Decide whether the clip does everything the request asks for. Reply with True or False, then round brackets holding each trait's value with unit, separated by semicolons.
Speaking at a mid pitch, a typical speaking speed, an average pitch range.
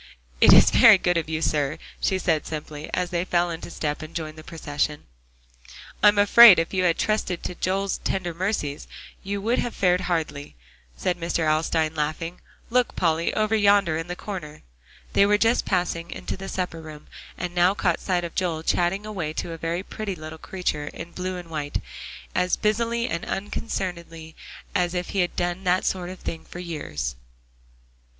True (175 Hz; 180 wpm; 3.0 semitones)